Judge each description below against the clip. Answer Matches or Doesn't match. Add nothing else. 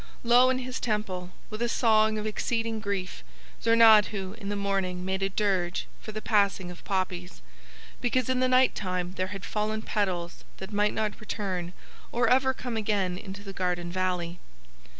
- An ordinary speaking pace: Matches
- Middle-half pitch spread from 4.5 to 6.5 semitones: Doesn't match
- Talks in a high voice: Matches